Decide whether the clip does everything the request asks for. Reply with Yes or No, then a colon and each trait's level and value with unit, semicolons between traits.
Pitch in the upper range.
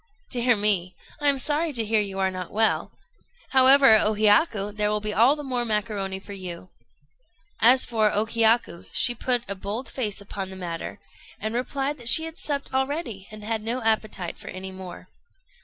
Yes: high, 220 Hz